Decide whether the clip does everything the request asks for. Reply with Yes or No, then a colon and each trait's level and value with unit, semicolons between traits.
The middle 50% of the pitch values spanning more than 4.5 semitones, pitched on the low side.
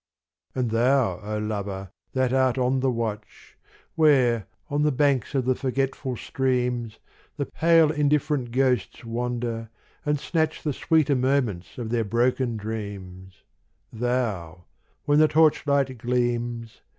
No: average, 3.4 semitones; low, 125 Hz